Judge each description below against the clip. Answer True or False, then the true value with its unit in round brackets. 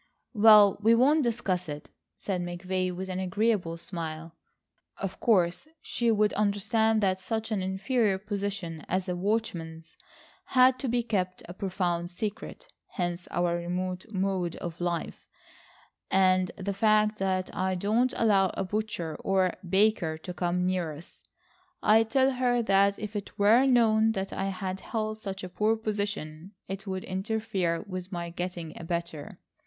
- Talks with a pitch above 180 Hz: True (190 Hz)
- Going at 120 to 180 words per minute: True (155 wpm)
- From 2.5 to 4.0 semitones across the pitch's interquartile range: True (3.3 semitones)